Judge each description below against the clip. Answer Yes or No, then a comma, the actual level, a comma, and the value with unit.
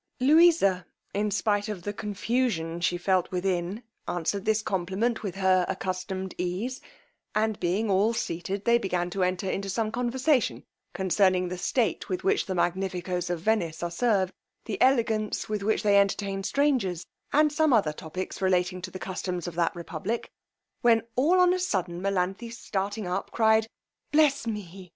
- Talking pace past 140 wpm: Yes, average, 160 wpm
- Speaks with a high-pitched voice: Yes, high, 195 Hz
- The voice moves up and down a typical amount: Yes, average, 3.8 semitones